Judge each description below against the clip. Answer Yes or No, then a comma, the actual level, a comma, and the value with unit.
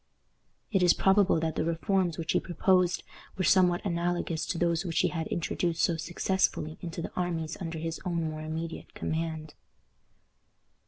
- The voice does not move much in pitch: Yes, narrow, 1.7 semitones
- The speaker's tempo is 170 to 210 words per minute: No, average, 160 wpm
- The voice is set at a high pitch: No, medium, 170 Hz